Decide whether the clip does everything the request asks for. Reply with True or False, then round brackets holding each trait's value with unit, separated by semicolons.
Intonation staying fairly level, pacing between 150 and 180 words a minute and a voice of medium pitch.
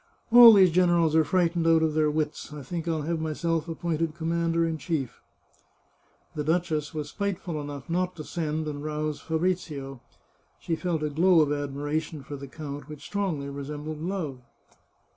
True (2.3 semitones; 165 wpm; 155 Hz)